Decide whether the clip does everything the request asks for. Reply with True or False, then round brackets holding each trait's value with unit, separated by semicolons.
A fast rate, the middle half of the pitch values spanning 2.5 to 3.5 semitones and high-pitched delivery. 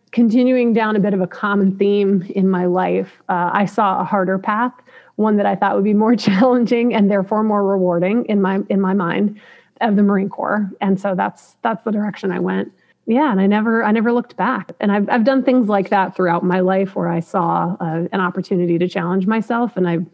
True (225 wpm; 2.8 semitones; 200 Hz)